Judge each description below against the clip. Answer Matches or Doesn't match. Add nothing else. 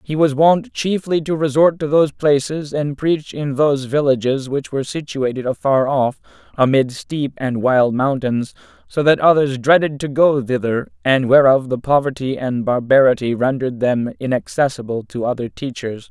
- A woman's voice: Doesn't match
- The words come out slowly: Doesn't match